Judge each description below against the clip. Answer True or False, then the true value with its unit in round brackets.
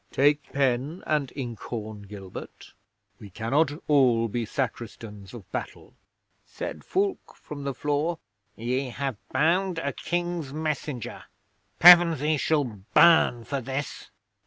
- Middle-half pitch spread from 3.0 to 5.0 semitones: True (4.7 semitones)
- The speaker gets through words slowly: True (120 wpm)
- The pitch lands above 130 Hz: True (140 Hz)